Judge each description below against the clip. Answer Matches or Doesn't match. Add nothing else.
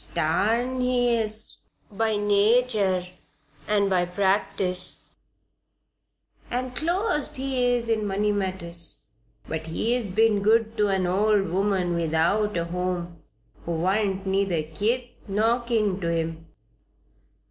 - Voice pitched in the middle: Doesn't match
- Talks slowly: Matches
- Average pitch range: Matches